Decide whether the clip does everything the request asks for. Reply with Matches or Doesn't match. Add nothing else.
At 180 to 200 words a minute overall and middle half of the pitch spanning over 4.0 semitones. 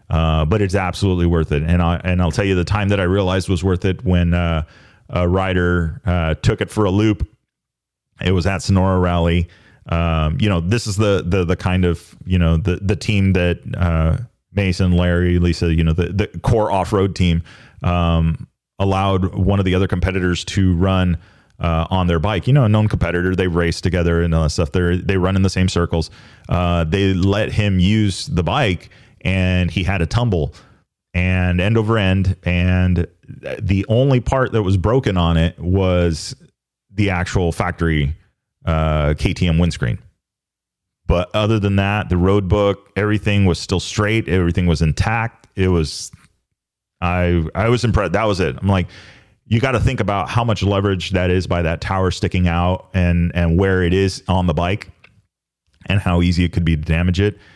Doesn't match